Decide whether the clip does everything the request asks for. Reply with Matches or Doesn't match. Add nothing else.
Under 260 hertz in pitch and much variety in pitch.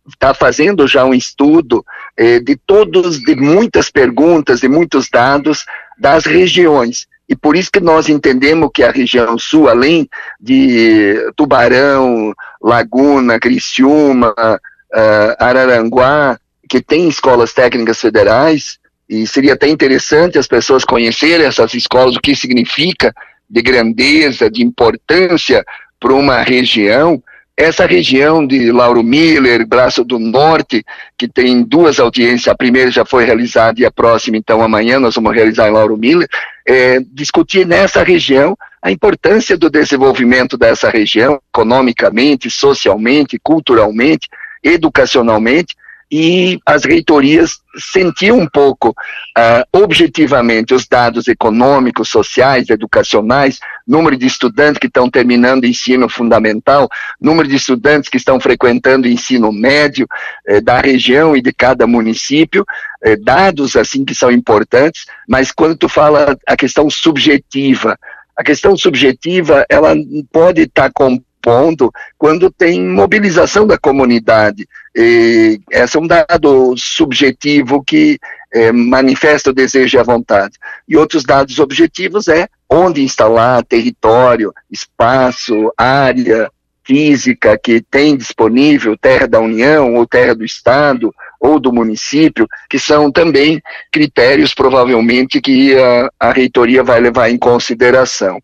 Matches